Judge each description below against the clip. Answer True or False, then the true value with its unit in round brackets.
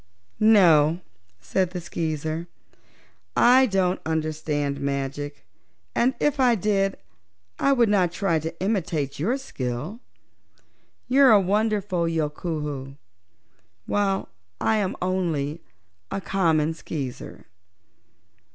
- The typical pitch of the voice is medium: True (170 Hz)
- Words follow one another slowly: True (105 wpm)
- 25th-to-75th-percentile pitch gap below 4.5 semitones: False (5.2 semitones)